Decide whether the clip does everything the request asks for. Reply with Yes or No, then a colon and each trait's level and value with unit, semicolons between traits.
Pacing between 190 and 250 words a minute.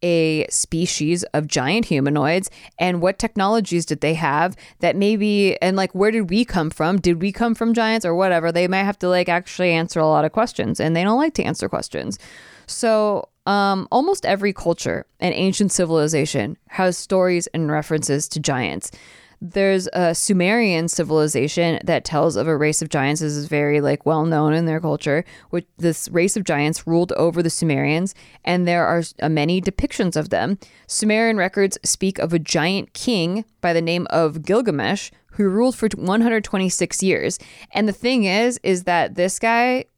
No: average, 180 wpm